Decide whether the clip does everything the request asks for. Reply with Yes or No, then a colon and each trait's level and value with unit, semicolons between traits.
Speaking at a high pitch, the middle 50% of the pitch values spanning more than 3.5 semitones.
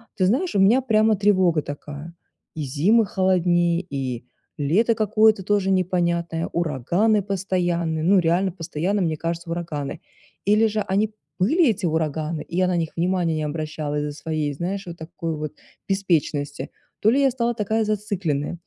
No: medium, 175 Hz; average, 4.4 semitones